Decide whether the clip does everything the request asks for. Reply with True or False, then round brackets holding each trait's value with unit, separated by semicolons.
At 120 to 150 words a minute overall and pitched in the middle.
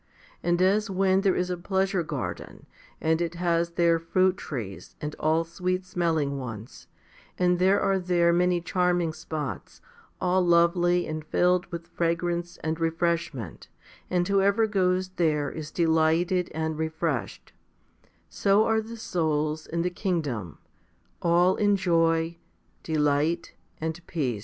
True (135 wpm; 170 Hz)